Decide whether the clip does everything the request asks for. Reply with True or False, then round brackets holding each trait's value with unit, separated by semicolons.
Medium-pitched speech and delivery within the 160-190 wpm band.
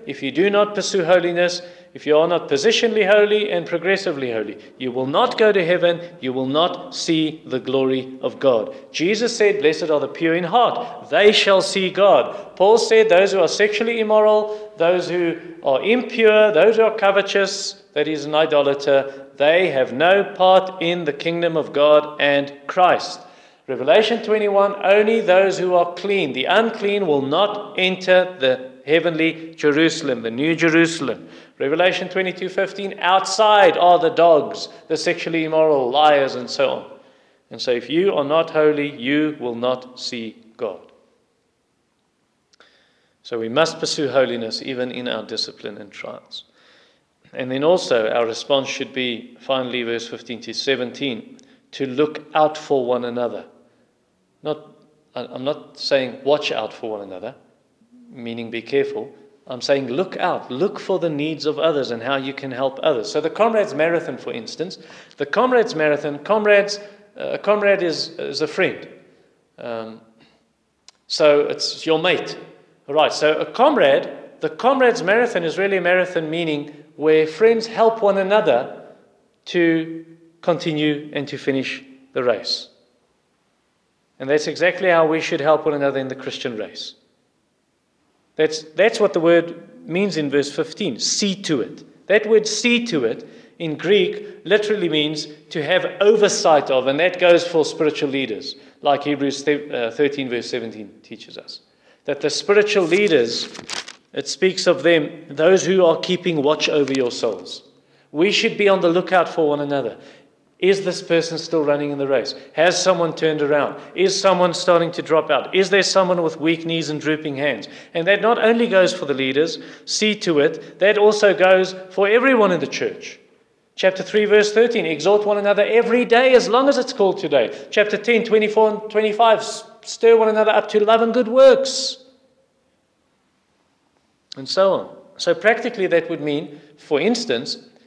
True (170 Hz; 165 wpm)